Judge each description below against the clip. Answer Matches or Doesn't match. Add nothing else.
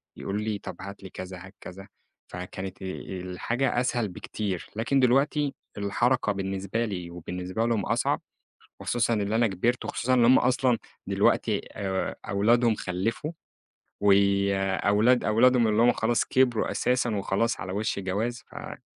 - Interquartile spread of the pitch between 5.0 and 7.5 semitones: Doesn't match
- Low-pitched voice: Matches